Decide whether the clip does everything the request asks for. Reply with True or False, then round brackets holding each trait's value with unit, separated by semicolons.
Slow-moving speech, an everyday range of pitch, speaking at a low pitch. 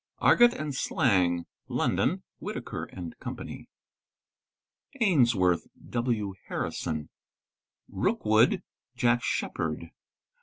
False (70 wpm; 7.0 semitones; 110 Hz)